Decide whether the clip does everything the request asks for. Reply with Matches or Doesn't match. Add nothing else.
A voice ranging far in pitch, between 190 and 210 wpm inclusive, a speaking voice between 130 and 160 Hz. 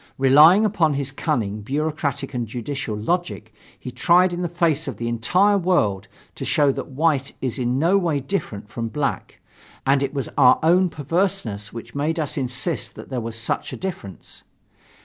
Doesn't match